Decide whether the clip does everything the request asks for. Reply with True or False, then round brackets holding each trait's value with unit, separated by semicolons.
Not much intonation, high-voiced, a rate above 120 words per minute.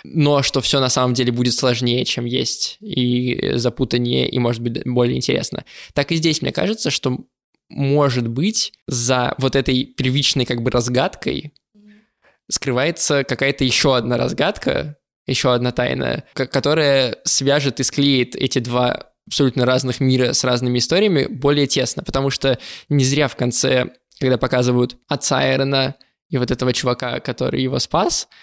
False (2.1 semitones; 130 Hz; 150 wpm)